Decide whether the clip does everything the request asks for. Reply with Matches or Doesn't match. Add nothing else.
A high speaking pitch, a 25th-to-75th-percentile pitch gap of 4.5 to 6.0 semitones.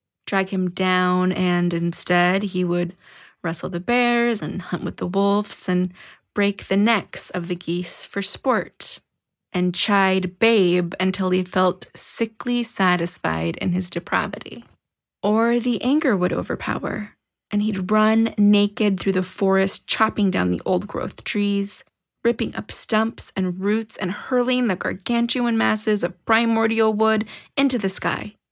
Doesn't match